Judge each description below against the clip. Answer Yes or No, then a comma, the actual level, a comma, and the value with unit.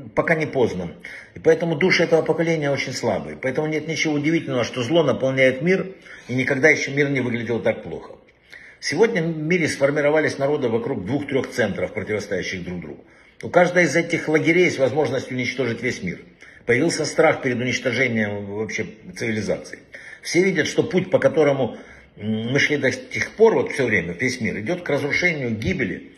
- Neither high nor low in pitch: Yes, medium, 150 Hz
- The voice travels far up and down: No, average, 4.1 semitones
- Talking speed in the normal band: No, fast, 165 wpm